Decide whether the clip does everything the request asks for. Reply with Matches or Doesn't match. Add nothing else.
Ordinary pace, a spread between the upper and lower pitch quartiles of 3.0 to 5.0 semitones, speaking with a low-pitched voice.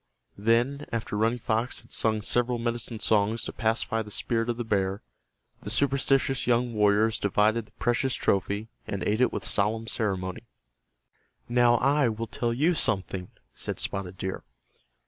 Doesn't match